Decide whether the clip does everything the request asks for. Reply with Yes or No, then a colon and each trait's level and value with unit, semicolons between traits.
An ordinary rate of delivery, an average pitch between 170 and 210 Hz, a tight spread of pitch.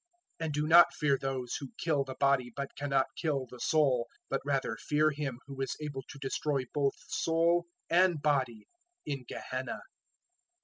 No: average, 170 wpm; medium, 140 Hz; narrow, 2.3 semitones